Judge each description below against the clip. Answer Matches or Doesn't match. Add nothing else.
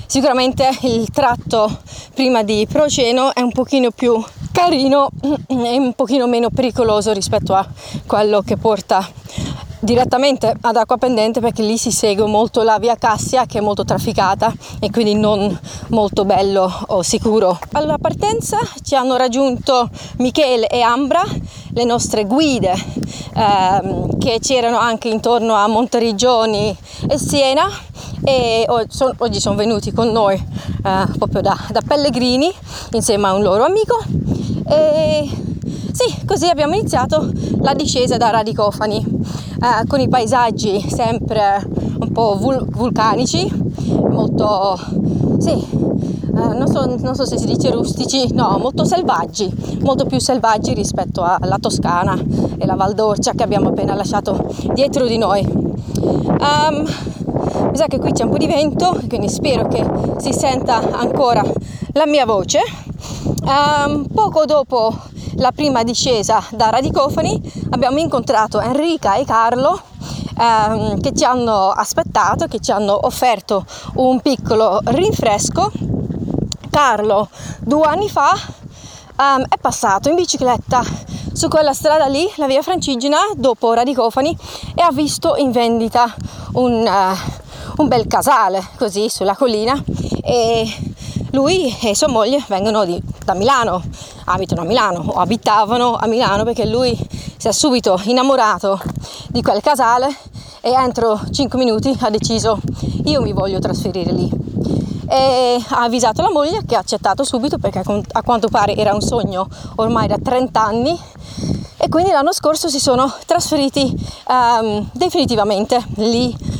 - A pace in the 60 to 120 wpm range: Doesn't match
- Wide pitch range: Doesn't match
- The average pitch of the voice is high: Matches